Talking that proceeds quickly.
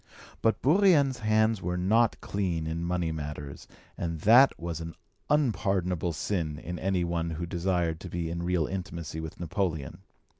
No: average, 155 wpm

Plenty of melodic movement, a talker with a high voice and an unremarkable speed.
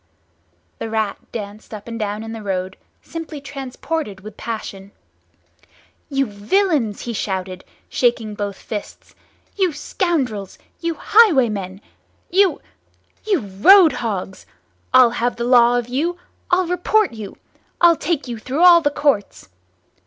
No: wide, 7.6 semitones; high, 240 Hz; slow, 120 wpm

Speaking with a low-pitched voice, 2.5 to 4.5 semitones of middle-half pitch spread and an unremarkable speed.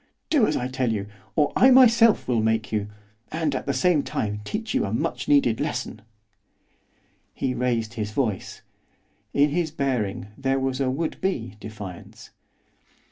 No: low, 130 Hz; average, 5.2 semitones; average, 160 wpm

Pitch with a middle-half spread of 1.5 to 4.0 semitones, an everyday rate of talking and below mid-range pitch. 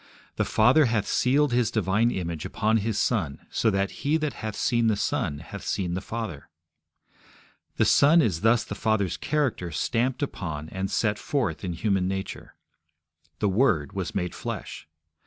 No: average, 4.6 semitones; average, 165 wpm; low, 105 Hz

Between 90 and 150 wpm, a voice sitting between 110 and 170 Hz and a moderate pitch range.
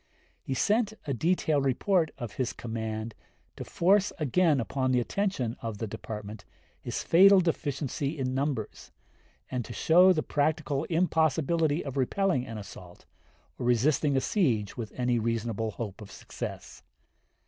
No: average, 145 wpm; low, 135 Hz; wide, 5.9 semitones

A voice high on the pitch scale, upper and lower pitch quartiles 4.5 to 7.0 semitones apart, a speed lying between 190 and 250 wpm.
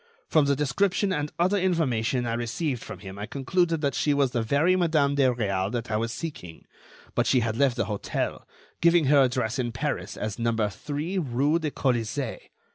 No: low, 135 Hz; average, 5.1 semitones; average, 195 wpm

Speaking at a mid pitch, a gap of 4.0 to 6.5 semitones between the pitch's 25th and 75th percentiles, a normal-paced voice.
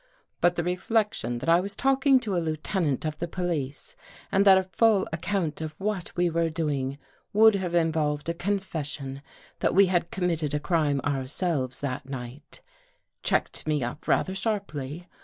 Yes: medium, 170 Hz; average, 4.5 semitones; average, 170 wpm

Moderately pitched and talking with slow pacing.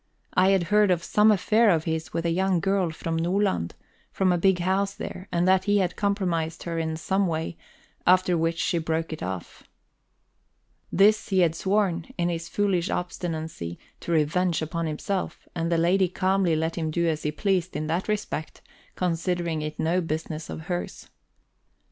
No: medium, 175 Hz; average, 180 wpm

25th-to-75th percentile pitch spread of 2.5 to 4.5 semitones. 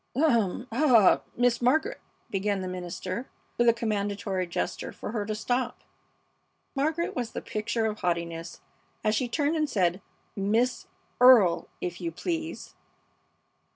No: average, 5.0 semitones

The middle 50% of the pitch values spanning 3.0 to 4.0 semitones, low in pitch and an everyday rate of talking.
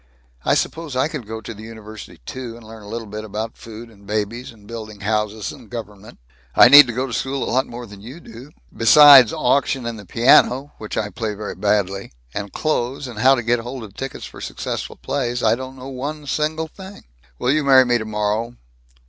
No: average, 3.5 semitones; low, 115 Hz; fast, 210 wpm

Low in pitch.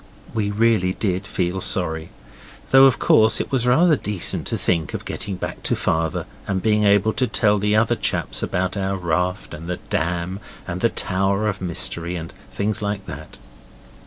Yes: very low, 95 Hz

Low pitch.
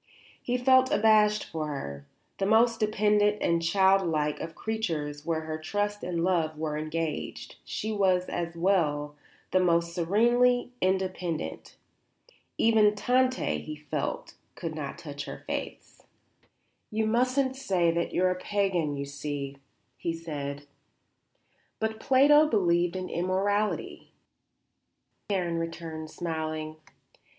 No: medium, 180 Hz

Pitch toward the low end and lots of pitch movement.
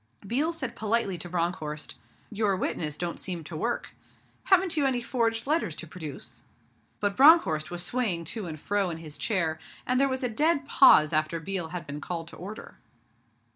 No: high, 190 Hz; wide, 7.1 semitones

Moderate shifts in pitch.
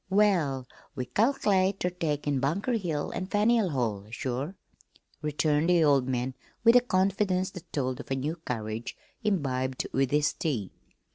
No: wide, 6.4 semitones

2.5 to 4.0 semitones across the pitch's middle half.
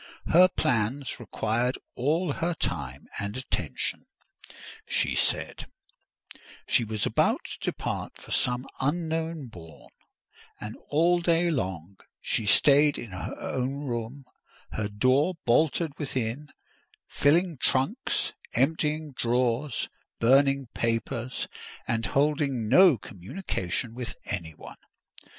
No: average, 5.2 semitones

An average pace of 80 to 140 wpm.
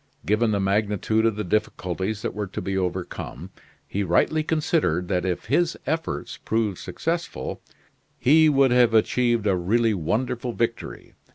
No: average, 150 wpm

